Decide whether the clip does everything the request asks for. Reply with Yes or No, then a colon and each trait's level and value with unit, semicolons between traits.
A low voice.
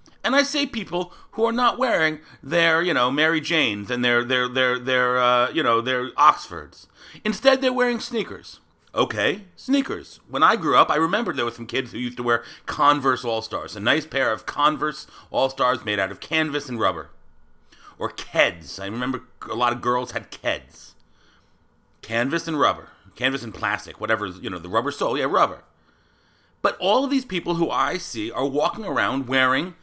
Yes: low, 130 Hz